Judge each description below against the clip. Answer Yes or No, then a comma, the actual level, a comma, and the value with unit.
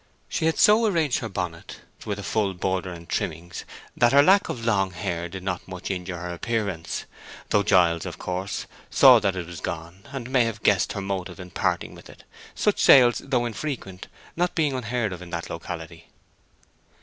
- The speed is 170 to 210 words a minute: Yes, average, 190 wpm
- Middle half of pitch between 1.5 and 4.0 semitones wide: No, average, 5.2 semitones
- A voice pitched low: Yes, very low, 95 Hz